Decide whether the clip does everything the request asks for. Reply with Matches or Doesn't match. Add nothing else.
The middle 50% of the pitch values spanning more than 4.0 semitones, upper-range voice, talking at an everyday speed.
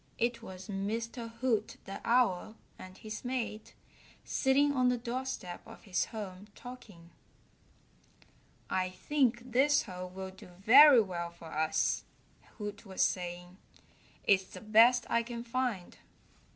Doesn't match